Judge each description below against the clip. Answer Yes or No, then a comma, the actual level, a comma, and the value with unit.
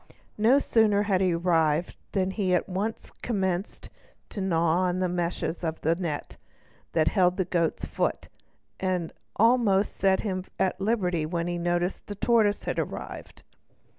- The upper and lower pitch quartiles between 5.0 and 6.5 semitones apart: No, average, 2.7 semitones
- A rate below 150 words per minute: Yes, average, 140 wpm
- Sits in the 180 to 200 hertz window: Yes, medium, 185 Hz